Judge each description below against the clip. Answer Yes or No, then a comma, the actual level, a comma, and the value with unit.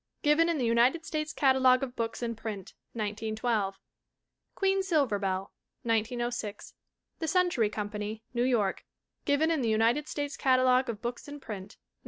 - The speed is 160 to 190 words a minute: No, average, 150 wpm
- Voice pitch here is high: Yes, high, 240 Hz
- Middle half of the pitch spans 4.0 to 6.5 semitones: Yes, average, 4.9 semitones